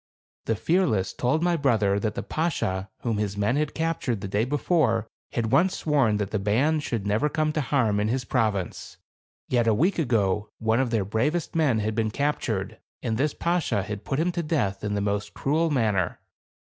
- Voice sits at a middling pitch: No, low, 115 Hz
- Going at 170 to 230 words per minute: Yes, average, 195 wpm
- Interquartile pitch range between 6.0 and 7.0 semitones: Yes, wide, 6.3 semitones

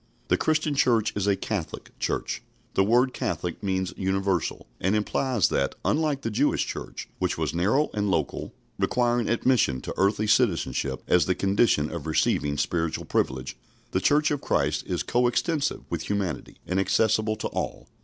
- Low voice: Yes, low, 105 Hz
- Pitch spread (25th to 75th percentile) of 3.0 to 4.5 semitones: No, average, 4.9 semitones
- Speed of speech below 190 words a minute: Yes, average, 160 wpm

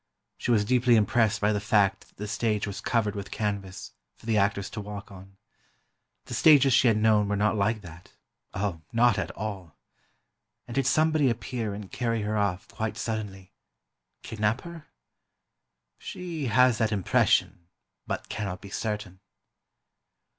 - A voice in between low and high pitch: No, low, 105 Hz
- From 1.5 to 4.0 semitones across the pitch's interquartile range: Yes, average, 2.8 semitones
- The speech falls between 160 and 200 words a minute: No, average, 150 wpm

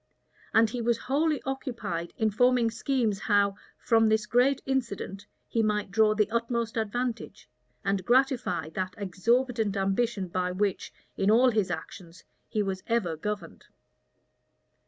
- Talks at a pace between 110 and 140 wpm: Yes, slow, 135 wpm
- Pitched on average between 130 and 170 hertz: No, high, 215 Hz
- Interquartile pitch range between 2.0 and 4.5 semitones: Yes, average, 3.6 semitones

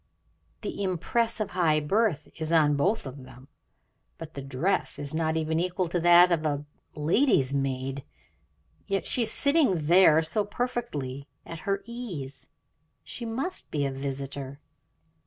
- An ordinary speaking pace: Yes, average, 150 wpm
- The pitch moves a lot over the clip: Yes, wide, 6.0 semitones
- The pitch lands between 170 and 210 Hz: No, medium, 160 Hz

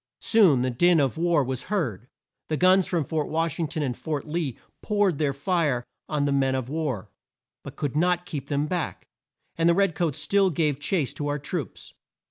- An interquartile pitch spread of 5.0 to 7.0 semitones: No, average, 3.8 semitones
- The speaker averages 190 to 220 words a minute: Yes, average, 200 wpm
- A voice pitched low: No, medium, 155 Hz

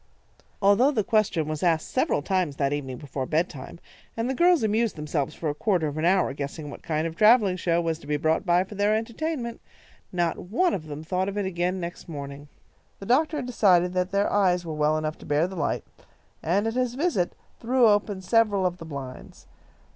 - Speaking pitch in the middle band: Yes, medium, 180 Hz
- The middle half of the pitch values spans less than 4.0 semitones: No, wide, 5.5 semitones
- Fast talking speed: Yes, fast, 215 wpm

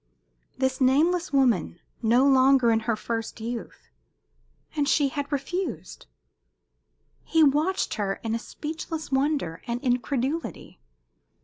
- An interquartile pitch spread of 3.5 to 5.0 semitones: Yes, average, 4.2 semitones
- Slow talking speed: Yes, slow, 115 wpm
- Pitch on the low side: No, very high, 265 Hz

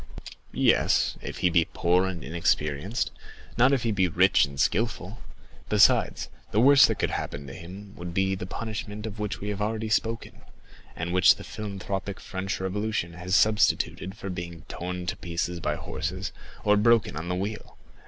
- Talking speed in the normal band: Yes, average, 175 wpm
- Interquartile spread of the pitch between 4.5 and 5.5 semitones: No, average, 3.4 semitones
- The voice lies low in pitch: Yes, very low, 95 Hz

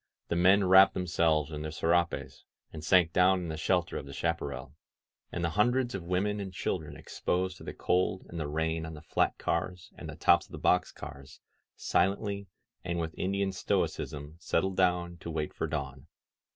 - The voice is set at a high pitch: No, very low, 85 Hz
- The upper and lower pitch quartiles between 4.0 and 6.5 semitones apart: No, average, 2.9 semitones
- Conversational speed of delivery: Yes, average, 190 wpm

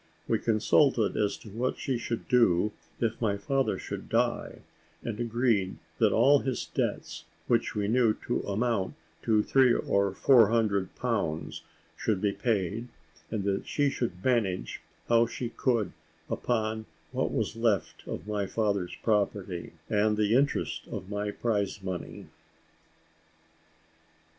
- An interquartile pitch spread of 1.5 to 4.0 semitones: Yes, average, 2.9 semitones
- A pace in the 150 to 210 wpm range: No, average, 140 wpm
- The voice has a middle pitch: No, low, 110 Hz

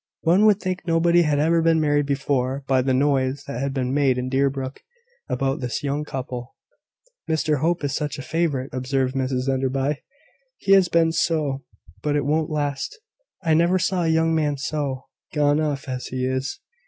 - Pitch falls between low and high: Yes, medium, 145 Hz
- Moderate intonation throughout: Yes, average, 3.2 semitones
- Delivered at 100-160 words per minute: No, average, 180 wpm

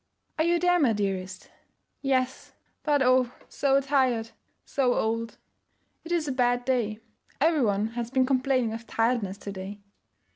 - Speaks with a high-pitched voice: Yes, very high, 250 Hz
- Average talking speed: Yes, average, 150 wpm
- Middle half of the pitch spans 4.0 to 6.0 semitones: No, average, 3.5 semitones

